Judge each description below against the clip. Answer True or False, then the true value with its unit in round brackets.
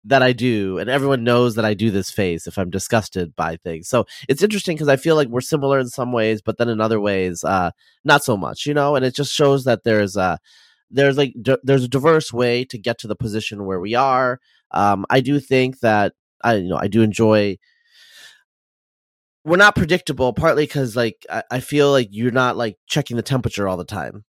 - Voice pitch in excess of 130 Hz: False (125 Hz)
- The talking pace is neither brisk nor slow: False (225 wpm)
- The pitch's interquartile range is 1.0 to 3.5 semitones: False (4.5 semitones)